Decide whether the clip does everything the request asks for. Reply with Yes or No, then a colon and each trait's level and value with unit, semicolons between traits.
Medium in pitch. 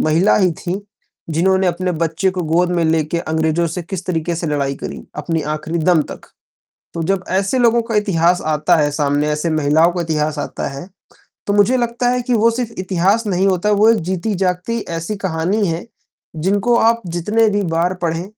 Yes: medium, 180 Hz